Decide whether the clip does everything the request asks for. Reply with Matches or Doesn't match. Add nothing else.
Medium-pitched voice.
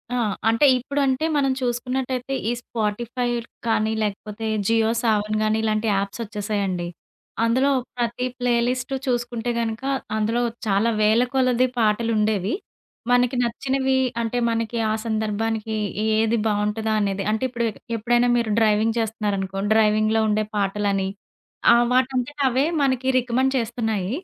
Doesn't match